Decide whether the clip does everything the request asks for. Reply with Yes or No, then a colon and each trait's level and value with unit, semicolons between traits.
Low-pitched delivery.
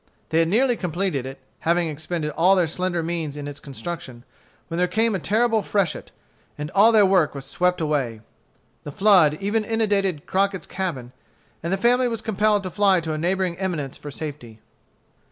No: medium, 180 Hz